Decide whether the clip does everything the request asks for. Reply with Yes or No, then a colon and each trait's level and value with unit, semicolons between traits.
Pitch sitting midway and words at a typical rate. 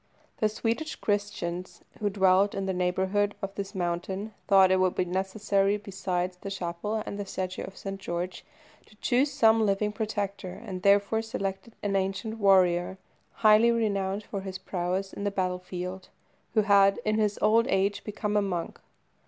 No: high, 195 Hz; average, 165 wpm